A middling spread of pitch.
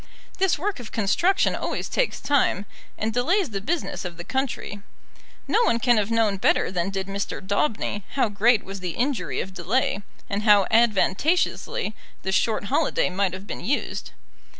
Yes: average, 4.9 semitones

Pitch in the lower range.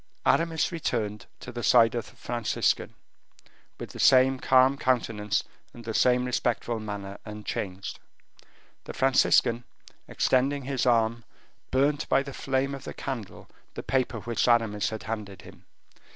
Yes: low, 120 Hz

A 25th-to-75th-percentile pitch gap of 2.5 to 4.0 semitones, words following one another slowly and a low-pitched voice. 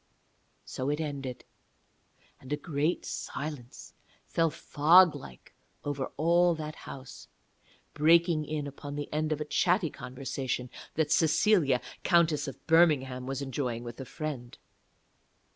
No: average, 3.2 semitones; slow, 125 wpm; medium, 150 Hz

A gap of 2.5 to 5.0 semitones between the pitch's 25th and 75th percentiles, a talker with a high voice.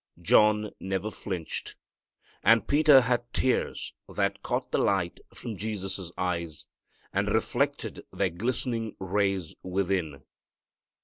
No: average, 3.8 semitones; low, 100 Hz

